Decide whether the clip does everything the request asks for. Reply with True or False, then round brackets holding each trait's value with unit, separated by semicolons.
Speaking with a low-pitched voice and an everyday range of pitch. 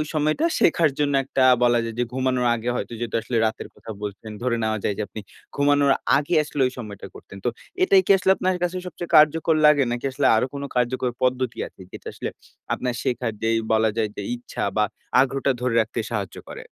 True (125 Hz; 4.2 semitones)